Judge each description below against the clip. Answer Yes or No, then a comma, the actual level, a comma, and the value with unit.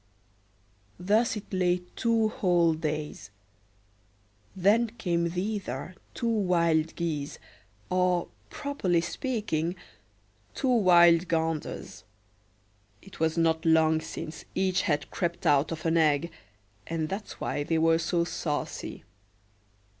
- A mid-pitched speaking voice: Yes, medium, 170 Hz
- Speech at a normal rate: No, slow, 110 wpm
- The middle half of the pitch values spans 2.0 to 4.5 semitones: Yes, average, 2.9 semitones